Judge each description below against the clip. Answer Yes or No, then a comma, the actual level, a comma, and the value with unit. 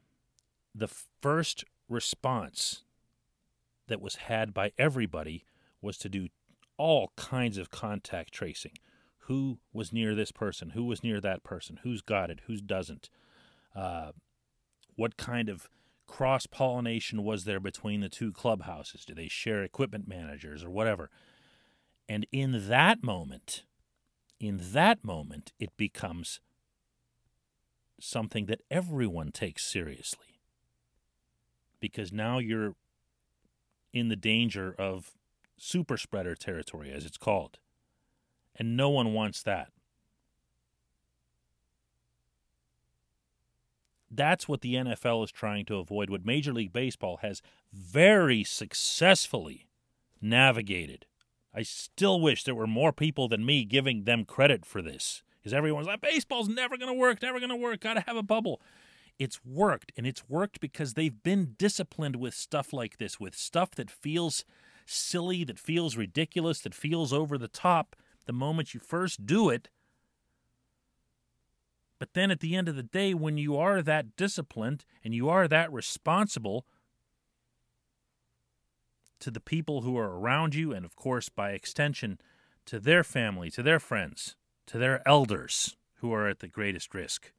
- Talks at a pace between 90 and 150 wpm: Yes, average, 140 wpm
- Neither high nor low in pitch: No, low, 115 Hz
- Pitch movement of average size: No, wide, 6.9 semitones